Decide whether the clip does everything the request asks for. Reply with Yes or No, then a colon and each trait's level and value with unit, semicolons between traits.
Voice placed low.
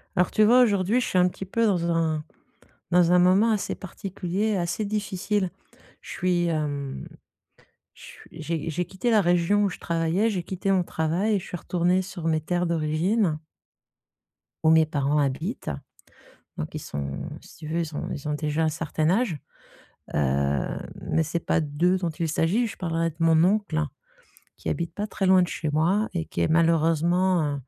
No: medium, 170 Hz